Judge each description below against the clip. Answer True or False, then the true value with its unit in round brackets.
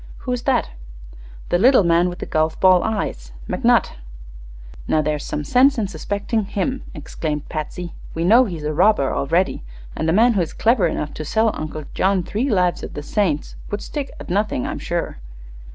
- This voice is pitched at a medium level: True (180 Hz)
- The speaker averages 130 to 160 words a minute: False (185 wpm)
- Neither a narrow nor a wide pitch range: False (5.9 semitones)